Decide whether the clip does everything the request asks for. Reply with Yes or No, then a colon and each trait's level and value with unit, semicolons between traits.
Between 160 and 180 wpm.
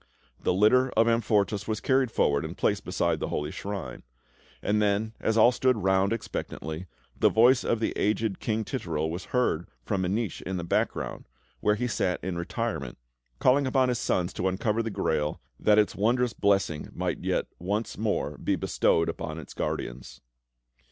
Yes: average, 175 wpm